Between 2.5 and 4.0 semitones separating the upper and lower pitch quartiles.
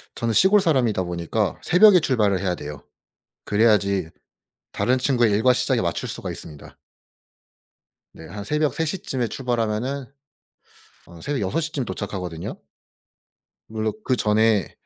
No: wide, 5.5 semitones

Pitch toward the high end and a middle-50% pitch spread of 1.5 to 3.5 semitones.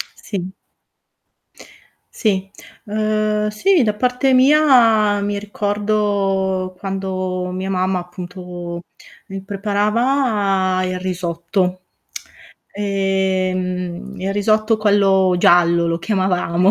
Yes: high, 195 Hz; narrow, 2.4 semitones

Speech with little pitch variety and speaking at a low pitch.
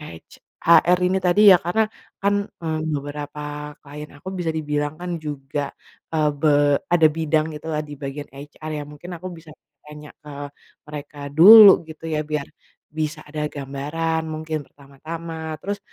No: narrow, 1.9 semitones; medium, 155 Hz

